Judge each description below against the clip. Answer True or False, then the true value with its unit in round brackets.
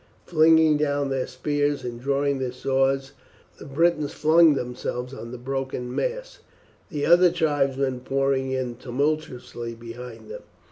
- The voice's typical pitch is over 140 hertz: False (135 Hz)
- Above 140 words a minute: False (135 wpm)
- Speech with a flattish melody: False (3.3 semitones)